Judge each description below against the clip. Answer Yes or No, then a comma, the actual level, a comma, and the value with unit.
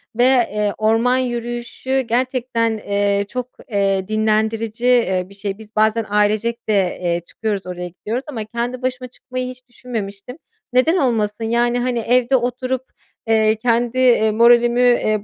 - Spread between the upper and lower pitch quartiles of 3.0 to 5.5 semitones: No, narrow, 2.6 semitones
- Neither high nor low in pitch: No, high, 230 Hz